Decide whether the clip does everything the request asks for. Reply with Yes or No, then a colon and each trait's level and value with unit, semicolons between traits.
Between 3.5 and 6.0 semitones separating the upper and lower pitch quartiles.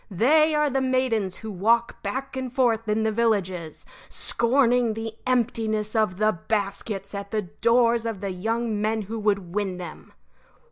No: average, 2.8 semitones